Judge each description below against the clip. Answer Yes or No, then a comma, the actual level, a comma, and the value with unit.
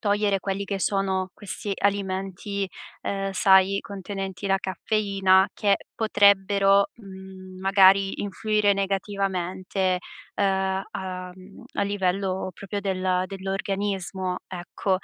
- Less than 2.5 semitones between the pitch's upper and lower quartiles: Yes, narrow, 1.1 semitones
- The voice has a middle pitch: No, high, 195 Hz